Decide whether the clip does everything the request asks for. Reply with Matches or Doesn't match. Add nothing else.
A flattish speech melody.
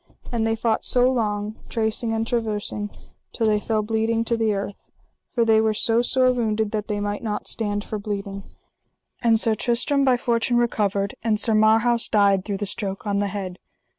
Matches